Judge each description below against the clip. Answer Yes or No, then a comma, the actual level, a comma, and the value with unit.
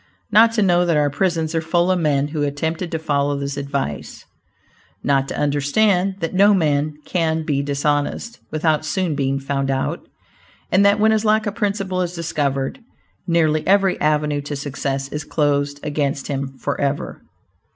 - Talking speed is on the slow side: No, average, 165 wpm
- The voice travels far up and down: No, average, 4.1 semitones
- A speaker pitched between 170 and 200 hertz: No, medium, 155 Hz